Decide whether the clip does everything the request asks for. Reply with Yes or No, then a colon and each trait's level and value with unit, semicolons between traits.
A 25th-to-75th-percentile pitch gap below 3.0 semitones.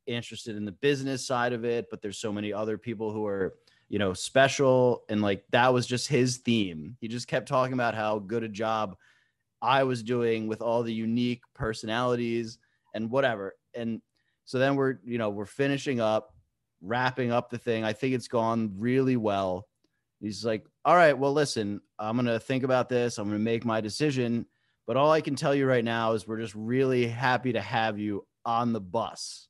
Yes: narrow, 2.6 semitones